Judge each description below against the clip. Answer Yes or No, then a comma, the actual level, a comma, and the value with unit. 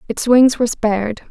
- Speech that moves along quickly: No, average, 185 wpm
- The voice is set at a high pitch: Yes, high, 235 Hz